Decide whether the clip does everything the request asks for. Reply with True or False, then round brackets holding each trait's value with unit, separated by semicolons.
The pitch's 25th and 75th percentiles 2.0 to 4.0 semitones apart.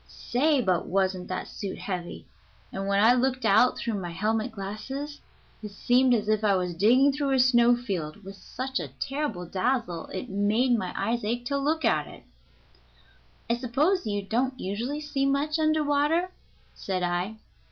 False (5.4 semitones)